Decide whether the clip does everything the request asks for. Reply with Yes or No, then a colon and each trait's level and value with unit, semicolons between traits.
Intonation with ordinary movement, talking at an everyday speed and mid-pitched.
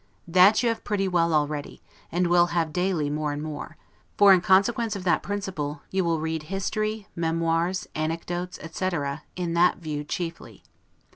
Yes: average, 3.1 semitones; average, 160 wpm; medium, 175 Hz